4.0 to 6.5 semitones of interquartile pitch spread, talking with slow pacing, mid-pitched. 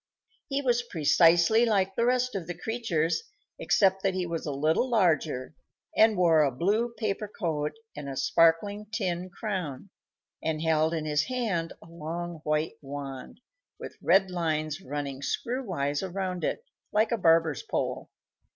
No: average, 5.2 semitones; average, 155 wpm; medium, 175 Hz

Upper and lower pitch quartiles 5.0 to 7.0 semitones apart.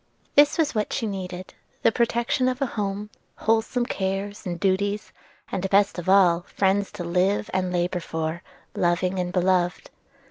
No: average, 2.8 semitones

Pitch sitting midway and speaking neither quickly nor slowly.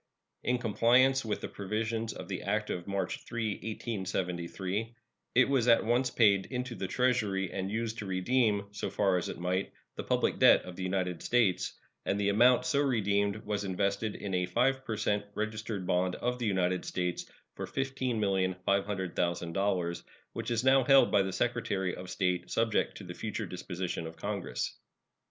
No: low, 100 Hz; average, 170 wpm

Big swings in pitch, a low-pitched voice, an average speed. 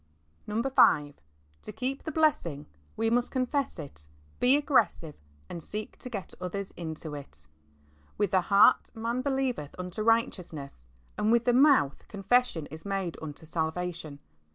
No: wide, 7.7 semitones; high, 195 Hz; average, 145 wpm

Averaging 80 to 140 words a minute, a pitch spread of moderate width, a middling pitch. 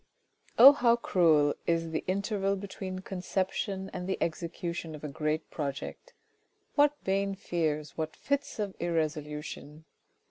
Yes: slow, 135 wpm; average, 4.1 semitones; medium, 175 Hz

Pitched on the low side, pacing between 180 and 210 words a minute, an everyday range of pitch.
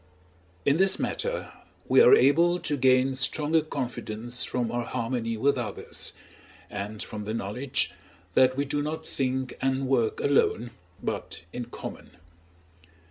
No: low, 130 Hz; slow, 135 wpm; average, 3.1 semitones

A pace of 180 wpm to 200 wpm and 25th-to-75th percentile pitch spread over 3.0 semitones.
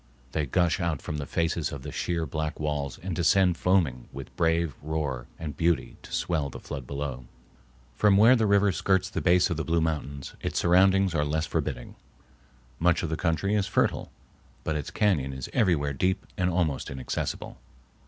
Yes: average, 185 wpm; average, 4.1 semitones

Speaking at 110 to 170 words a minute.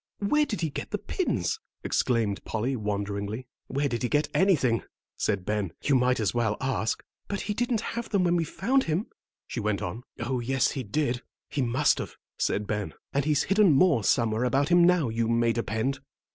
No: average, 195 wpm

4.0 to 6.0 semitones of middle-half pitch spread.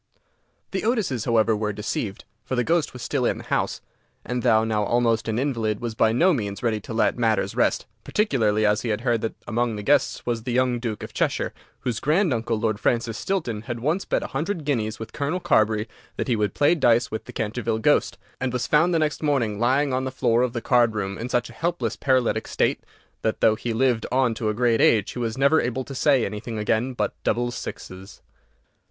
No: average, 3.1 semitones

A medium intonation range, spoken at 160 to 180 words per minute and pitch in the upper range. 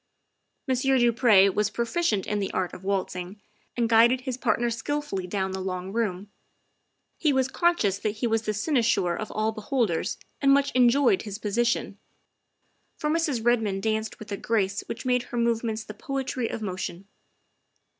Yes: average, 3.9 semitones; average, 175 wpm; high, 225 Hz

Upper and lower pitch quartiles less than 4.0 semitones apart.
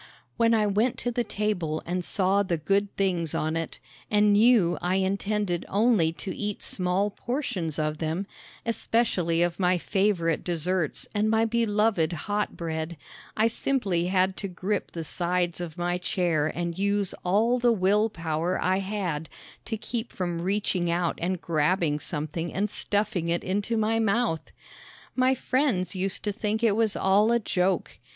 Yes: average, 3.6 semitones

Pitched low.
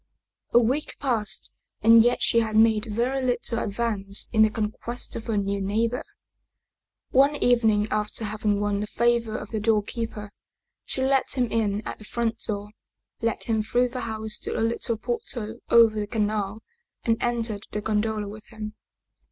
No: high, 220 Hz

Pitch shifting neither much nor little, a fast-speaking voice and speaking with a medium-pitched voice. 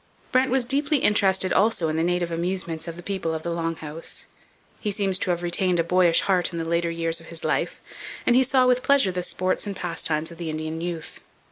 Yes: average, 3.1 semitones; fast, 230 wpm; medium, 175 Hz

